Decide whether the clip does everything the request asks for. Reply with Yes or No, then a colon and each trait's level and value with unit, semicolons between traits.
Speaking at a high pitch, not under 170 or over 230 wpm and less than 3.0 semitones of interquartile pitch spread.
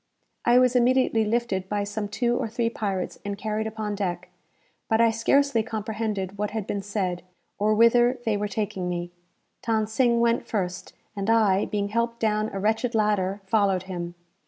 Yes: high, 215 Hz; average, 175 wpm; narrow, 2.5 semitones